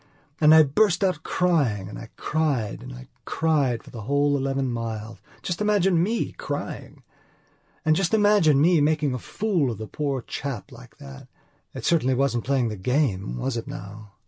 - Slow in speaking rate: No, average, 180 wpm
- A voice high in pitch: No, medium, 140 Hz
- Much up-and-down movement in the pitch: Yes, wide, 5.8 semitones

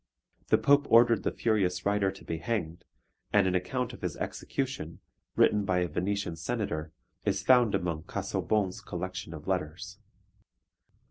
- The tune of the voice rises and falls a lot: No, average, 3.5 semitones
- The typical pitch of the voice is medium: No, very low, 95 Hz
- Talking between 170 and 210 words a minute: No, average, 145 wpm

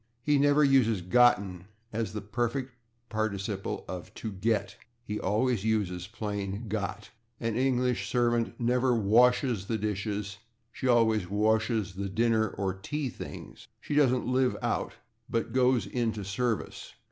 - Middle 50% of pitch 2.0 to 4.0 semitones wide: Yes, average, 3.5 semitones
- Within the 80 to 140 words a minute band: Yes, slow, 135 wpm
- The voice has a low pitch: Yes, low, 110 Hz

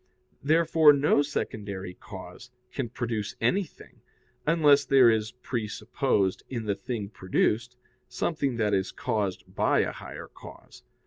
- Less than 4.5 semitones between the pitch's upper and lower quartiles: No, average, 5.3 semitones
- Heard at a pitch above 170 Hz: No, low, 115 Hz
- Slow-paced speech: Yes, slow, 125 wpm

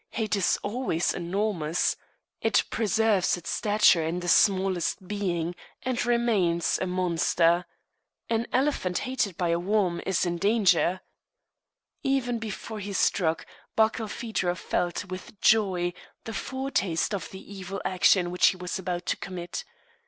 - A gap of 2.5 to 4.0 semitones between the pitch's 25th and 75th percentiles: Yes, average, 3.7 semitones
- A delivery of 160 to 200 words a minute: No, slow, 135 wpm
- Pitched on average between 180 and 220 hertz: Yes, high, 190 Hz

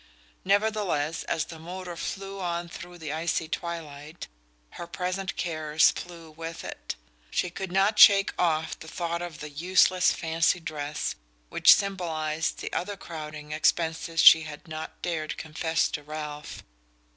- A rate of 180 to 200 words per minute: No, average, 145 wpm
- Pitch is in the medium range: Yes, medium, 165 Hz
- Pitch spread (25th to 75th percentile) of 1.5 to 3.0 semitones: Yes, narrow, 2.4 semitones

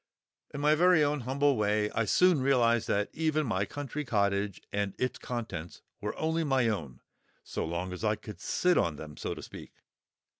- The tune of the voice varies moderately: No, wide, 6.4 semitones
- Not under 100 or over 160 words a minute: No, average, 185 wpm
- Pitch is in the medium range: No, low, 115 Hz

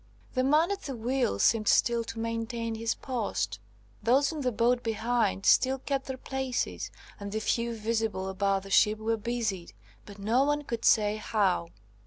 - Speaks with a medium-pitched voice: No, high, 230 Hz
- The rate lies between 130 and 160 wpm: No, average, 175 wpm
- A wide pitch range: No, average, 3.4 semitones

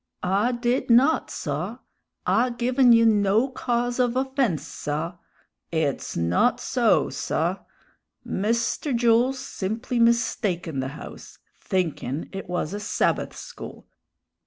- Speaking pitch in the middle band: No, high, 230 Hz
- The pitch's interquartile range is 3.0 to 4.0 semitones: No, average, 5.3 semitones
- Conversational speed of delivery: No, slow, 115 wpm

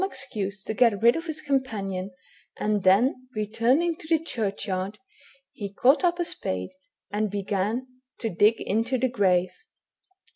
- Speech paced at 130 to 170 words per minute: Yes, average, 145 wpm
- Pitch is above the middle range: Yes, high, 220 Hz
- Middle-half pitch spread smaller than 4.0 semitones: No, average, 4.8 semitones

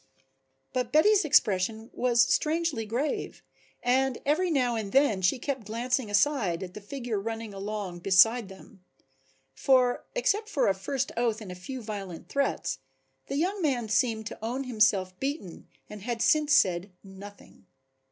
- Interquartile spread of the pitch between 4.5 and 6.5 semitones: Yes, average, 5.3 semitones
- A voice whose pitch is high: Yes, high, 230 Hz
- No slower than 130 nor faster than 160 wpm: Yes, average, 150 wpm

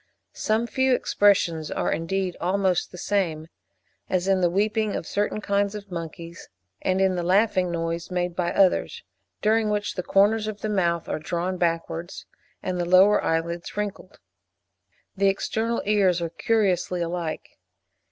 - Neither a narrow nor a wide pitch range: Yes, average, 3.1 semitones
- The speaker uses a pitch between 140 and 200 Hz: Yes, medium, 185 Hz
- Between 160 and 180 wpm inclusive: No, average, 150 wpm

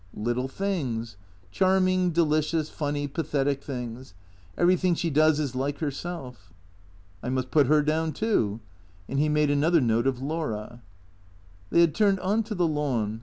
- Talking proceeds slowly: No, average, 155 wpm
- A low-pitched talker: No, medium, 145 Hz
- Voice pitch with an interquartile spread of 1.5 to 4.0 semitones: No, average, 5.0 semitones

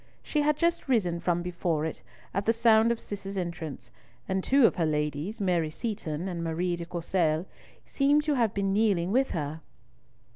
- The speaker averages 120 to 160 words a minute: No, average, 180 wpm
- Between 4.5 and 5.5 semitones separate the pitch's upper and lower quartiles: Yes, average, 5.2 semitones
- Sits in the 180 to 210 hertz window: Yes, medium, 185 Hz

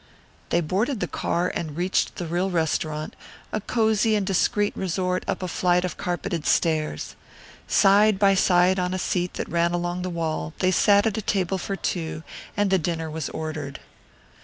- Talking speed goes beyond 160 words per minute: Yes, average, 180 wpm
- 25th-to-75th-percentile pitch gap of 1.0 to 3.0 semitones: Yes, average, 2.7 semitones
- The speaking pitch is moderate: Yes, medium, 180 Hz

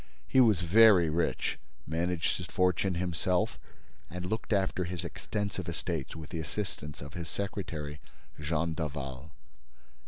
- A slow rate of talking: Yes, slow, 130 wpm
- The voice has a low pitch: Yes, very low, 85 Hz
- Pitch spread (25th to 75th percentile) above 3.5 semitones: No, average, 3.0 semitones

